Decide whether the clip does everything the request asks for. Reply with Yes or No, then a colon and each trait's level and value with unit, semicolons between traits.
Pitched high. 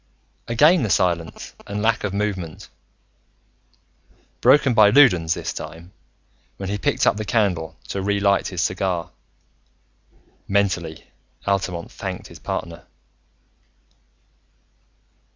No: low, 100 Hz